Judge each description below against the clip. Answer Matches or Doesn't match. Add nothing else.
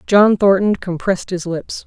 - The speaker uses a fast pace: Doesn't match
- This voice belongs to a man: Doesn't match